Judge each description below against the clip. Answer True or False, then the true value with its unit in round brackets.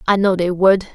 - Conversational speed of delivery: False (255 wpm)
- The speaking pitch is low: False (185 Hz)